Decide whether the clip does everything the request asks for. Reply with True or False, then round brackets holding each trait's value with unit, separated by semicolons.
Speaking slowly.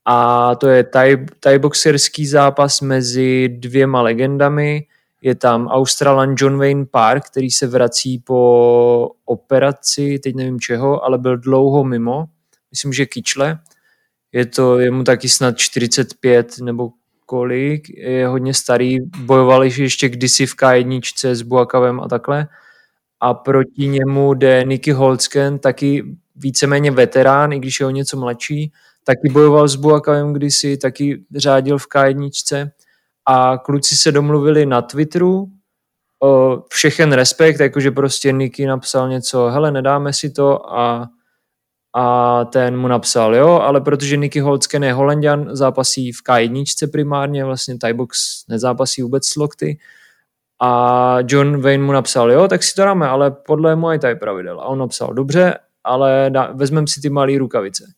False (150 wpm)